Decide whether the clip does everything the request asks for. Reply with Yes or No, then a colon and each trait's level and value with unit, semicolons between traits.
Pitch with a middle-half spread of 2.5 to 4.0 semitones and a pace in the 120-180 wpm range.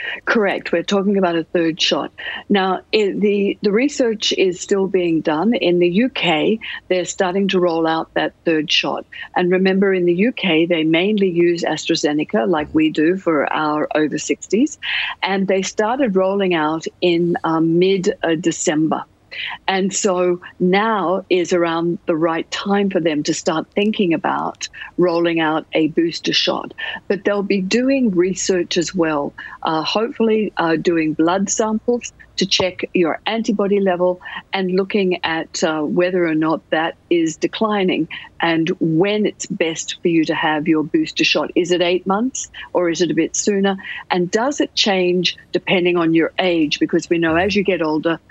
Yes: average, 3.5 semitones; average, 165 wpm